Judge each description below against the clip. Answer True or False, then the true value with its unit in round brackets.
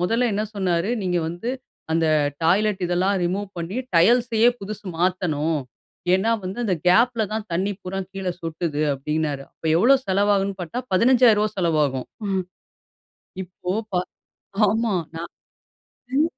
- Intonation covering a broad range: False (4.1 semitones)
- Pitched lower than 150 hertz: False (190 Hz)